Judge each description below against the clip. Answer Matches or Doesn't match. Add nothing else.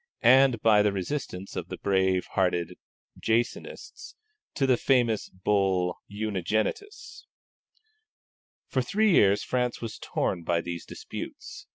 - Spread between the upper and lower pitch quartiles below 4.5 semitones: Doesn't match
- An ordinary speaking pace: Doesn't match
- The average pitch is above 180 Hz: Doesn't match